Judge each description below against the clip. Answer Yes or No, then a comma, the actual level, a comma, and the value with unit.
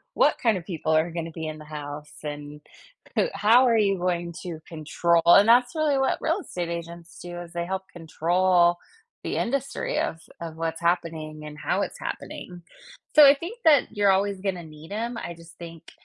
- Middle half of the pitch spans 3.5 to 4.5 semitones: Yes, average, 4.2 semitones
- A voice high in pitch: No, medium, 175 Hz